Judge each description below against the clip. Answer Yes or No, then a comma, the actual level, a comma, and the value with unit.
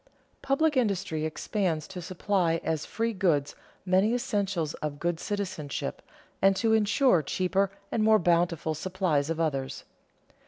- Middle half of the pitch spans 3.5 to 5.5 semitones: Yes, average, 4.2 semitones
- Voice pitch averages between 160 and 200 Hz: Yes, medium, 185 Hz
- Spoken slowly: Yes, slow, 130 wpm